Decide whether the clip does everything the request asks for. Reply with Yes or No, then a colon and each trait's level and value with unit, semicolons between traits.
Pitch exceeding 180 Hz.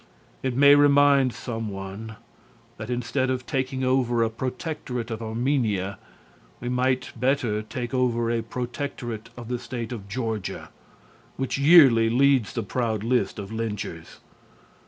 No: low, 120 Hz